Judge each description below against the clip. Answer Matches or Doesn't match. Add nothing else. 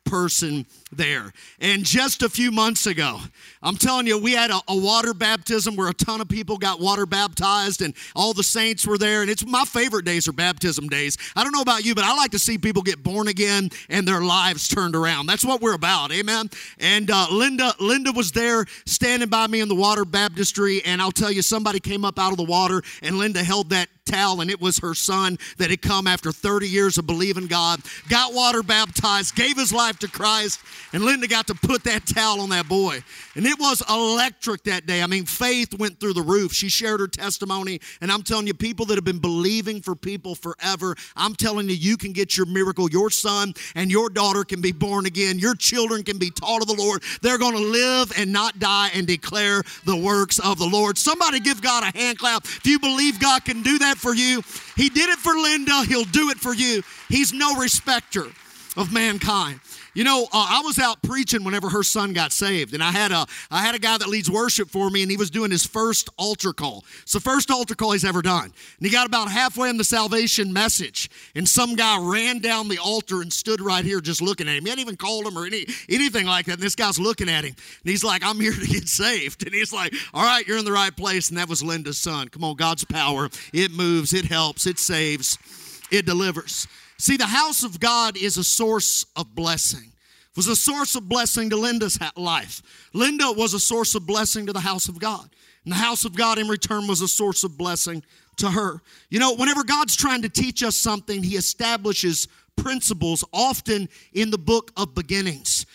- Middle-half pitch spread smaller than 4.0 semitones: Matches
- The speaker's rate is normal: Doesn't match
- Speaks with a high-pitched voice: Matches